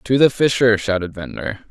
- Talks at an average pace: Yes, average, 175 wpm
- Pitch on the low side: Yes, low, 115 Hz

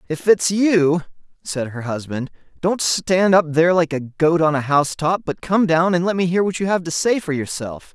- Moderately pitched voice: Yes, medium, 165 Hz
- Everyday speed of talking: No, fast, 235 wpm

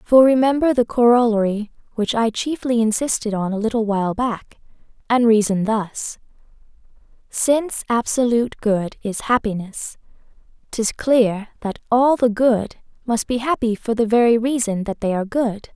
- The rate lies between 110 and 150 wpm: Yes, average, 145 wpm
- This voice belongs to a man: No, female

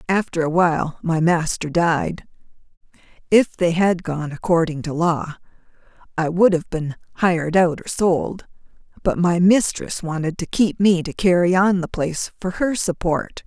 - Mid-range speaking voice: Yes, medium, 175 Hz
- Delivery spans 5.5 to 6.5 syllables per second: No, 4.4 syllables/s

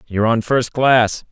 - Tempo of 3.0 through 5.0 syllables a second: Yes, 4.4 syllables/s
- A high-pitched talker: No, low, 115 Hz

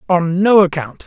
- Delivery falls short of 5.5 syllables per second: Yes, 4.6 syllables/s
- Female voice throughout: No, male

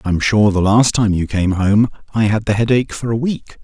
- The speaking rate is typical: No, fast, 250 wpm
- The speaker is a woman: No, male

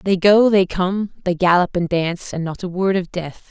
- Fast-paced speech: Yes, fast, 240 wpm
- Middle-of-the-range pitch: Yes, medium, 180 Hz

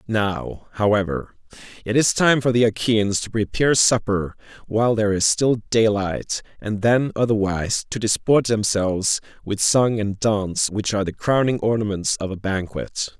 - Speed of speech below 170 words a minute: Yes, average, 155 wpm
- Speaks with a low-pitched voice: Yes, low, 105 Hz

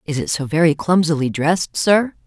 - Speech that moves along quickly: No, average, 185 wpm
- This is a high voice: No, medium, 160 Hz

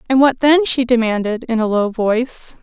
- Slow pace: No, fast, 205 wpm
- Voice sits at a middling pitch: No, high, 240 Hz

